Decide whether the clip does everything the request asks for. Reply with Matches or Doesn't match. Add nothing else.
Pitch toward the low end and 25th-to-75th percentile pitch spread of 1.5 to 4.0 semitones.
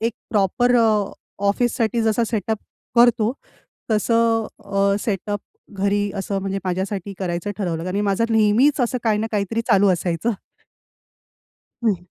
Doesn't match